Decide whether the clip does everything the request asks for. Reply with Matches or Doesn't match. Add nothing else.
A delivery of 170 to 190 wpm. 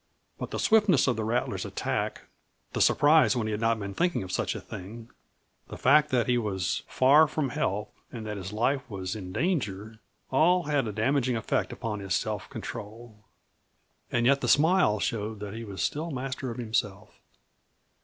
Matches